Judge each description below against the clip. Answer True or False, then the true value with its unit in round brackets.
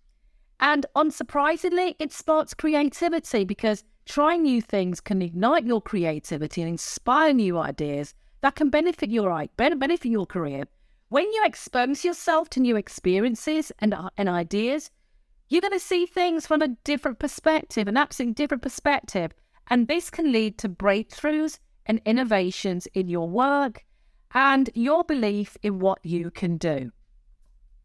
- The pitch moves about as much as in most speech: False (8.1 semitones)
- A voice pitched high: True (245 Hz)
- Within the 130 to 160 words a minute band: True (140 wpm)